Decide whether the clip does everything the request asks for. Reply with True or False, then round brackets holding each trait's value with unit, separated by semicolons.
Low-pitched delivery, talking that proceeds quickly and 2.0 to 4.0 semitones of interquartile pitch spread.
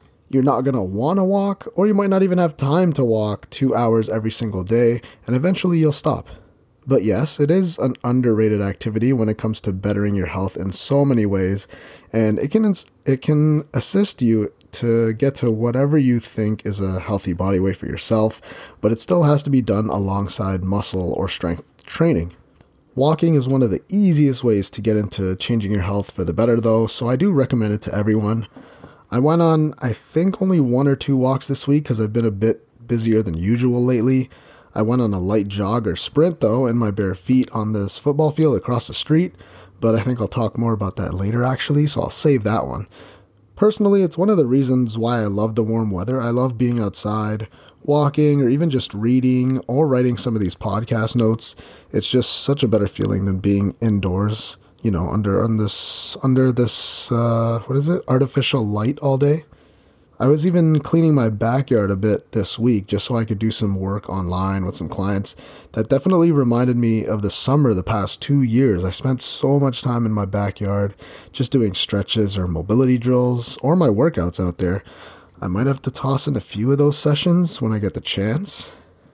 False (115 Hz; 210 wpm; 5.0 semitones)